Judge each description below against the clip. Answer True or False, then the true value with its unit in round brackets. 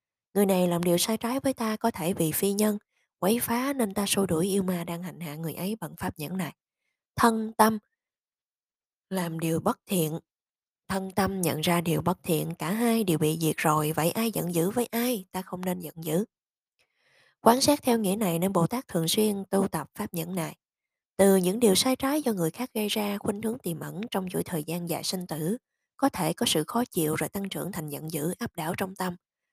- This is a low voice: False (185 Hz)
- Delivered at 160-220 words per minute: False (230 wpm)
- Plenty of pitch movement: False (4.8 semitones)